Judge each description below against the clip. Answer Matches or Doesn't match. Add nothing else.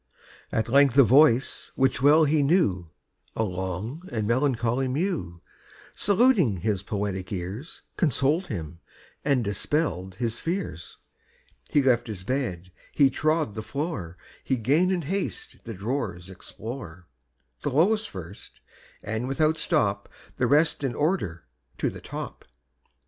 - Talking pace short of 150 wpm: Matches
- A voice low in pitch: Matches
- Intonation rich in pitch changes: Matches